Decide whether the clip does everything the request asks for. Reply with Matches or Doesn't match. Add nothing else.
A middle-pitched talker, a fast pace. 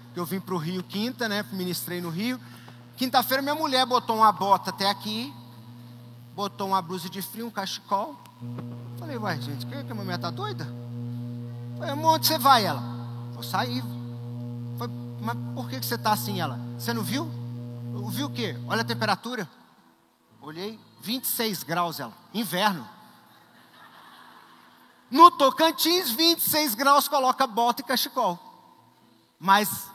Matches